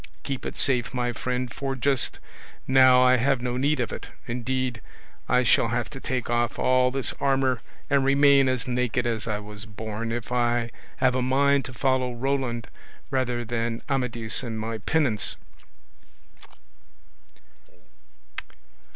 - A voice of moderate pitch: No, low, 125 Hz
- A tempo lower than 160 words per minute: Yes, average, 145 wpm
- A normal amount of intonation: No, narrow, 2.0 semitones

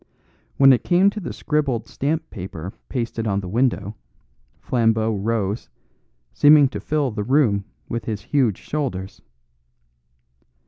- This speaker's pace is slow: Yes, slow, 130 wpm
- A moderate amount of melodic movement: No, wide, 5.7 semitones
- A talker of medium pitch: No, low, 115 Hz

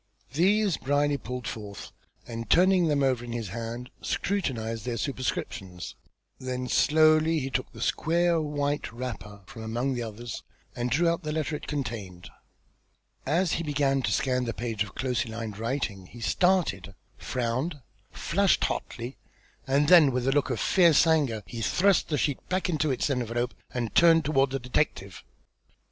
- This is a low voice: Yes, low, 130 Hz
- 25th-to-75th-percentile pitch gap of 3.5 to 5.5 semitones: Yes, average, 5.1 semitones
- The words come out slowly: No, average, 160 wpm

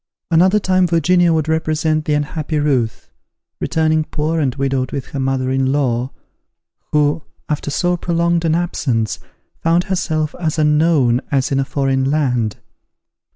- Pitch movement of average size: Yes, average, 3.5 semitones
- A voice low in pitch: No, medium, 150 Hz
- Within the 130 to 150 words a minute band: Yes, average, 145 wpm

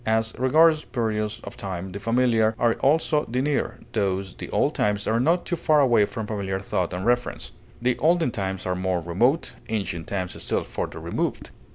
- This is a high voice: No, low, 110 Hz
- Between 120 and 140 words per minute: No, average, 185 wpm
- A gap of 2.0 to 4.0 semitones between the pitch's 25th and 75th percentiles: No, average, 4.8 semitones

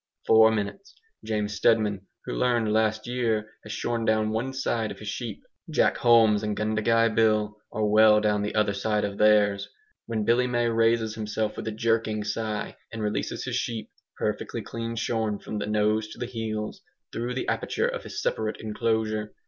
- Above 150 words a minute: Yes, average, 180 wpm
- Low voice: Yes, low, 110 Hz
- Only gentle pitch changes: Yes, narrow, 1.3 semitones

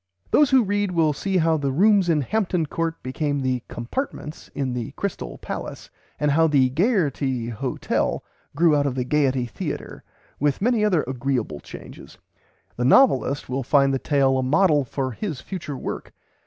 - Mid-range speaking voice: Yes, medium, 145 Hz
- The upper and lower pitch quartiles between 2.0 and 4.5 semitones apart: No, average, 5.0 semitones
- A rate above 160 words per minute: Yes, average, 170 wpm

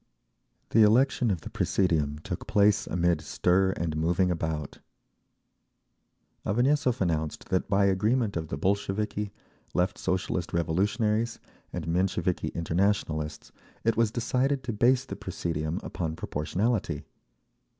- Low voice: Yes, very low, 95 Hz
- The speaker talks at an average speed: No, slow, 120 wpm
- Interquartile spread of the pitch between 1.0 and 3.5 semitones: No, average, 4.6 semitones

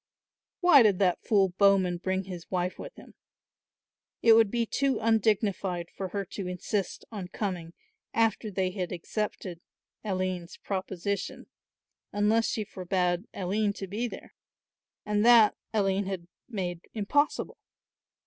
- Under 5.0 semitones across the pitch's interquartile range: Yes, average, 2.8 semitones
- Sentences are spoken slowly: Yes, slow, 130 wpm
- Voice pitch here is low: No, high, 195 Hz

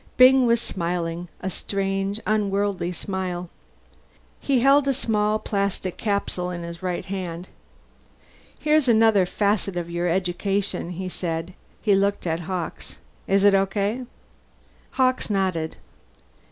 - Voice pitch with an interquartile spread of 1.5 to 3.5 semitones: Yes, average, 3.0 semitones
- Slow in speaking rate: Yes, slow, 125 wpm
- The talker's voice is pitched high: Yes, high, 195 Hz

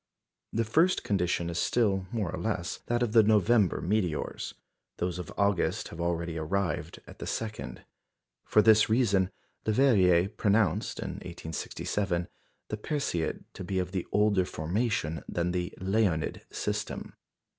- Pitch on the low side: Yes, very low, 95 Hz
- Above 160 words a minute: No, slow, 135 wpm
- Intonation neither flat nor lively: Yes, average, 3.9 semitones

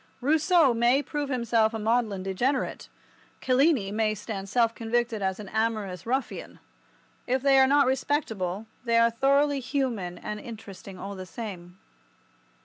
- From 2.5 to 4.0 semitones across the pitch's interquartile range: No, average, 4.5 semitones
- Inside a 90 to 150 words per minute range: Yes, average, 140 wpm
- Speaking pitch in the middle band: No, high, 230 Hz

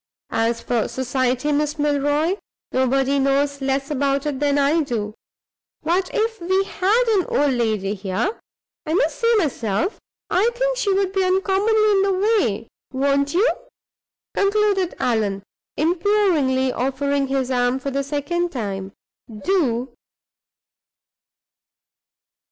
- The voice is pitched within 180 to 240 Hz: No, very high, 285 Hz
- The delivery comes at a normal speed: No, slow, 125 wpm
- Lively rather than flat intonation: Yes, wide, 6.6 semitones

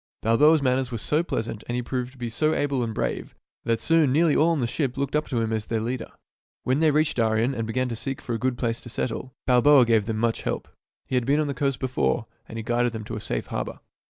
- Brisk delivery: Yes, fast, 265 wpm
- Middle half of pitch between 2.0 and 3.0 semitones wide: No, average, 3.4 semitones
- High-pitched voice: No, low, 125 Hz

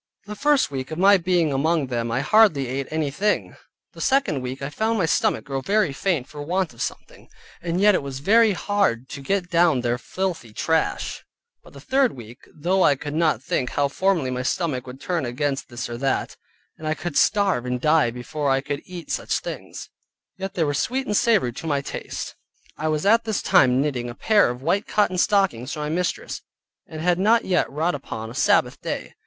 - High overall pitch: No, medium, 155 Hz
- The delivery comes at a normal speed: No, fast, 210 wpm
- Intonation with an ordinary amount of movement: No, wide, 6.3 semitones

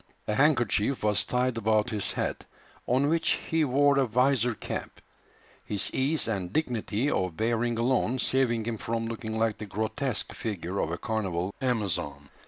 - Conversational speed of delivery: Yes, average, 160 wpm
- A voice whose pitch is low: Yes, low, 115 Hz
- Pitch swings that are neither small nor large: Yes, average, 3.5 semitones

